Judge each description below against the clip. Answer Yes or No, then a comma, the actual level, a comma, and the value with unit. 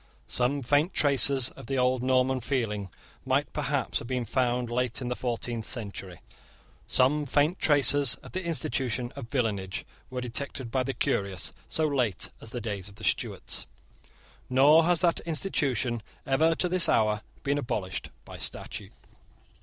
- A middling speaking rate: Yes, average, 155 wpm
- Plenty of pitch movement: No, average, 3.6 semitones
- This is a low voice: Yes, low, 125 Hz